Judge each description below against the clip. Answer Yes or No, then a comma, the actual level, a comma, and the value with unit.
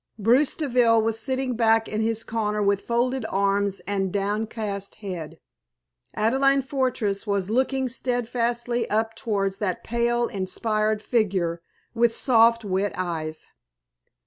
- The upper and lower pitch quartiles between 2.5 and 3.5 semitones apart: Yes, average, 3.1 semitones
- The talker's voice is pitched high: Yes, high, 220 Hz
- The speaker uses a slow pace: Yes, slow, 120 wpm